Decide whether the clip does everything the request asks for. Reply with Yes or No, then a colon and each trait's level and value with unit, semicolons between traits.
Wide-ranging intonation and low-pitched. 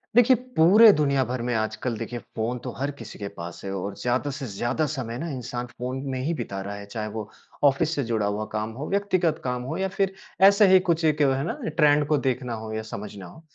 Yes: wide, 6.0 semitones; low, 130 Hz